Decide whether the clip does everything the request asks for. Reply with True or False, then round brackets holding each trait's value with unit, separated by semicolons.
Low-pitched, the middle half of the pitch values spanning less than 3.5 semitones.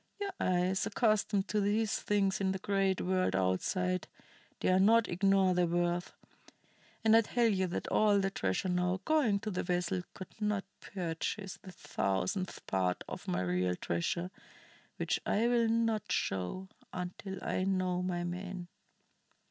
False (185 Hz; 2.6 semitones)